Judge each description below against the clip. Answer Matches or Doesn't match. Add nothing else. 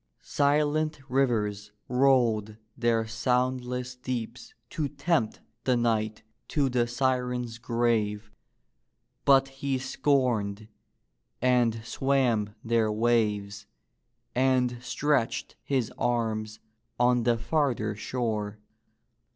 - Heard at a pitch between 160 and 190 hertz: Doesn't match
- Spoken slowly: Matches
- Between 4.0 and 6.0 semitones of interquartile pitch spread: Doesn't match